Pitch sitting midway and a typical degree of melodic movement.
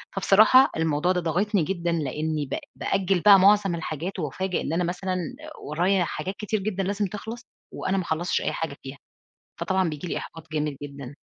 Yes: medium, 180 Hz; average, 3.8 semitones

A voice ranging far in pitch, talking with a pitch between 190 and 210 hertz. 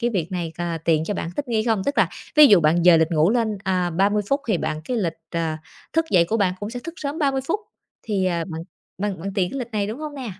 Yes: wide, 5.9 semitones; high, 200 Hz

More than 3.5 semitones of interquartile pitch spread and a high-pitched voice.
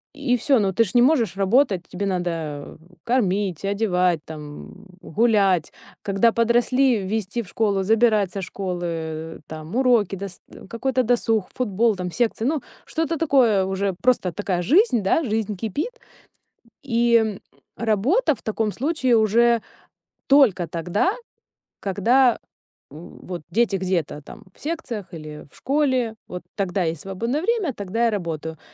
Yes: average, 4.9 semitones; high, 210 Hz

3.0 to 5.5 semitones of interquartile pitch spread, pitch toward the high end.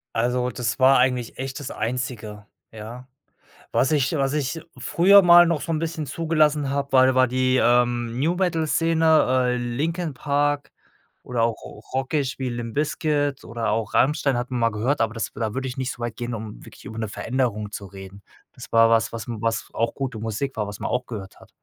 No: average, 4.0 semitones; low, 125 Hz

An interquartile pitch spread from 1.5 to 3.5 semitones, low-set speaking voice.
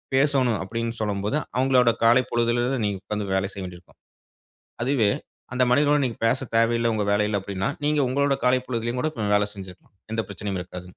No: average, 4.0 semitones; low, 115 Hz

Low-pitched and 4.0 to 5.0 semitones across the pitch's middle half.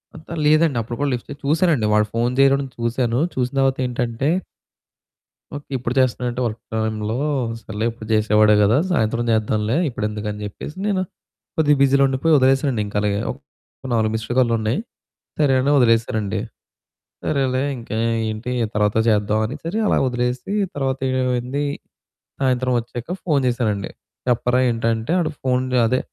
No: low, 120 Hz; average, 3.5 semitones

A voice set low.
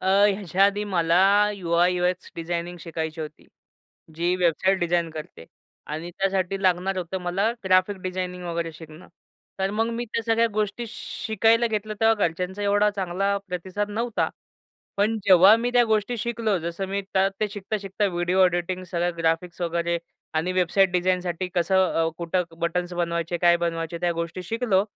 No: medium, 185 Hz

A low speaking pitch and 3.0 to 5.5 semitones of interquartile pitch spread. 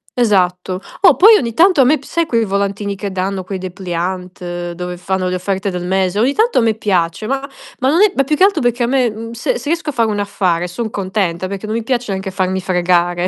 No: high, 200 Hz; average, 4.9 semitones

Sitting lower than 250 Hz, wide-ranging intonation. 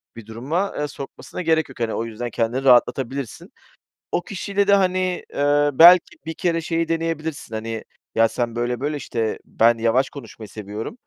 Yes: low, 135 Hz; wide, 6.2 semitones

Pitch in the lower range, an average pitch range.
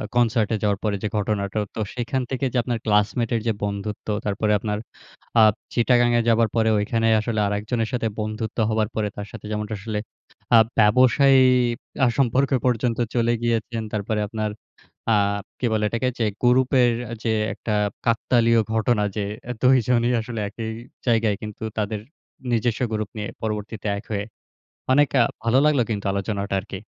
No: low, 110 Hz; narrow, 2.2 semitones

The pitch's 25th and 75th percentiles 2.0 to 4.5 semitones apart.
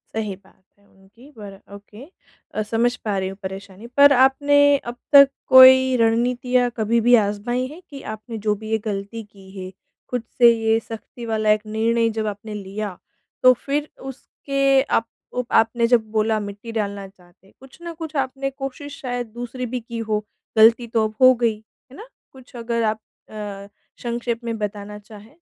Yes: average, 3.3 semitones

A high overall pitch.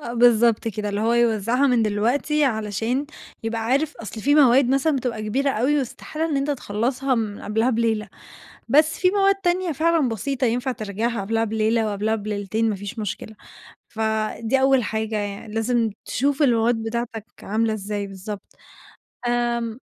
Yes: high, 230 Hz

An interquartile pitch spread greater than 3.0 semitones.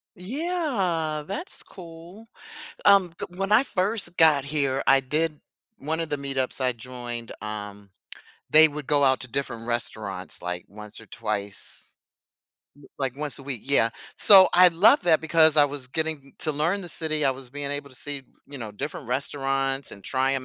Yes: average, 4.3 semitones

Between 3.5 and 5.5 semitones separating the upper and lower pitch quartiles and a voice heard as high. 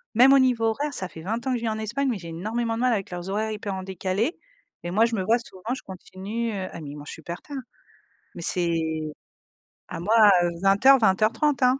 Yes: average, 4.1 semitones; high, 215 Hz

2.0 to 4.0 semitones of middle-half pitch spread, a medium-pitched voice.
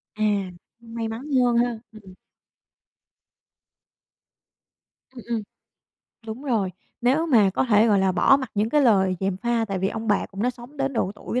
No: average, 3.4 semitones; high, 225 Hz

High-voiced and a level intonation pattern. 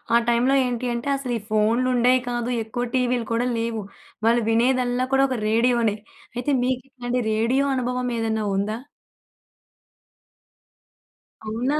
Yes: high, 245 Hz; narrow, 1.7 semitones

